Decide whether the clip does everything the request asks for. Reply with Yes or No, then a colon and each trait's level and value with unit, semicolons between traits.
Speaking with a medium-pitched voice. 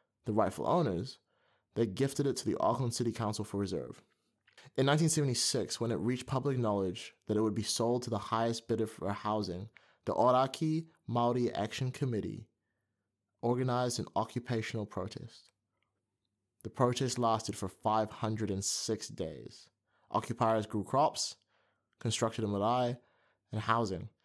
No: low, 115 Hz